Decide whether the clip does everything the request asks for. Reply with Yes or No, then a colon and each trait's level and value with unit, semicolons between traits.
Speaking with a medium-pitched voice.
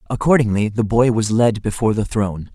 No: low, 110 Hz